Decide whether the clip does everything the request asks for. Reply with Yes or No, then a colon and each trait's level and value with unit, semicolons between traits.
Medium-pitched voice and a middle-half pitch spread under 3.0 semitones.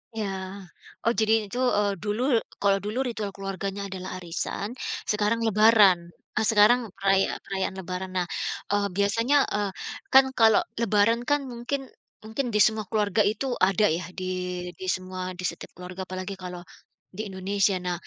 No: high, 205 Hz; narrow, 2.5 semitones